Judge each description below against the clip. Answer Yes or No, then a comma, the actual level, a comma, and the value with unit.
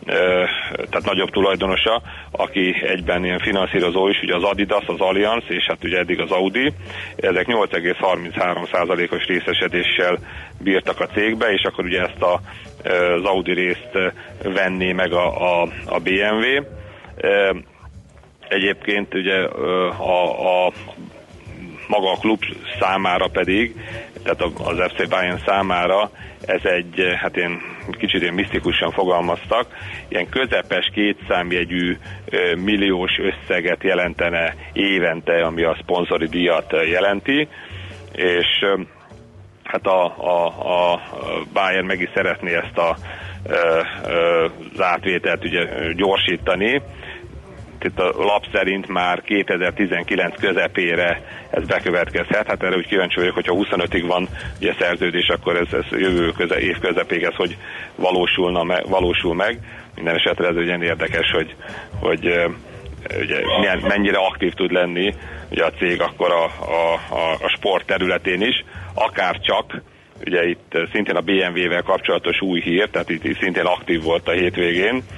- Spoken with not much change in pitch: Yes, narrow, 1.9 semitones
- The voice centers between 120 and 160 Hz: No, very low, 90 Hz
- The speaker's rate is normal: Yes, average, 125 wpm